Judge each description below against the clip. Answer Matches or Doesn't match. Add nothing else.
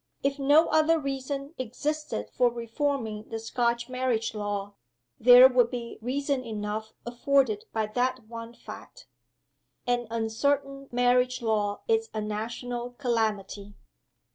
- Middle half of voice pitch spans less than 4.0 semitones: Matches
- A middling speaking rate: Doesn't match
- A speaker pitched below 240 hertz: Doesn't match